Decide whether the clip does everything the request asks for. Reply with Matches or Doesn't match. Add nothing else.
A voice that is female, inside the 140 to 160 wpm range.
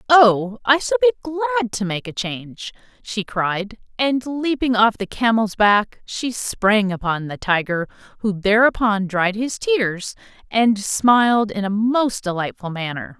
Matches